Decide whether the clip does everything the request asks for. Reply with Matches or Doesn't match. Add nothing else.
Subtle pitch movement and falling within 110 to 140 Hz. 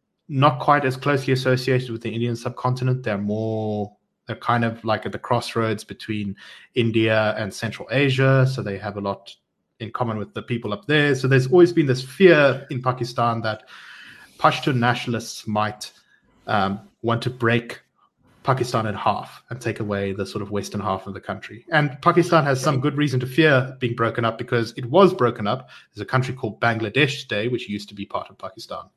Doesn't match